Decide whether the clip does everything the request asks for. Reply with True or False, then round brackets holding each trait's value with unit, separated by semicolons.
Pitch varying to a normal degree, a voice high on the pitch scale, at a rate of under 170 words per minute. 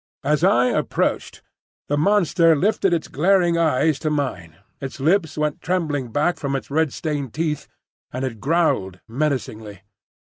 False (4.0 semitones; 150 Hz; 145 wpm)